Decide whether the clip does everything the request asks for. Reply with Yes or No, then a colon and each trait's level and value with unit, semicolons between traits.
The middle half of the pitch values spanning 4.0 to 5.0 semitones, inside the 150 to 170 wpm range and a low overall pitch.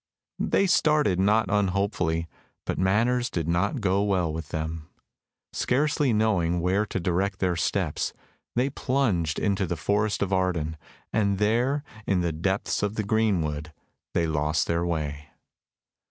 No: average, 4.3 semitones; average, 140 wpm; very low, 95 Hz